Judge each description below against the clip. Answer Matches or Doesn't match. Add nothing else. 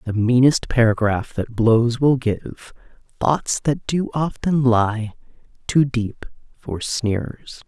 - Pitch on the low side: Matches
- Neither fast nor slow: Doesn't match